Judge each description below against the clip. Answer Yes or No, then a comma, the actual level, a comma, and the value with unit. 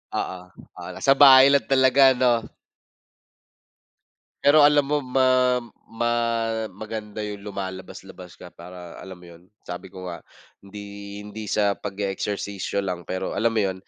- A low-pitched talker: Yes, low, 100 Hz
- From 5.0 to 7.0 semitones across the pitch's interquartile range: Yes, average, 5.3 semitones